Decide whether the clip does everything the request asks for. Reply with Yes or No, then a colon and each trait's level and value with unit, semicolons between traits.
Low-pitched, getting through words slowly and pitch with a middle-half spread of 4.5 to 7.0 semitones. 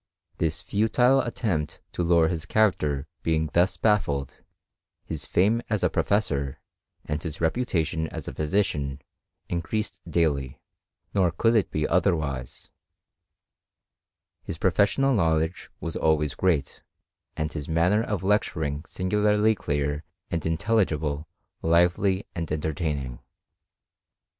Yes: very low, 85 Hz; slow, 120 wpm; average, 5.0 semitones